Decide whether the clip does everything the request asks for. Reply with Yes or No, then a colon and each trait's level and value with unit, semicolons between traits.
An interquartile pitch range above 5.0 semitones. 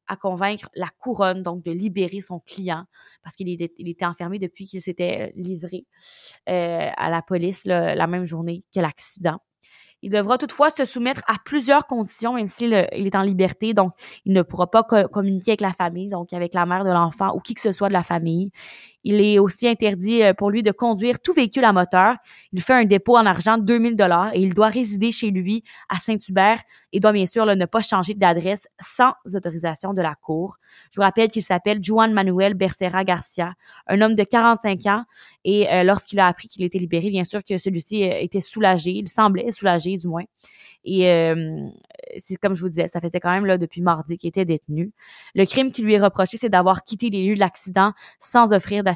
No: average, 3.2 semitones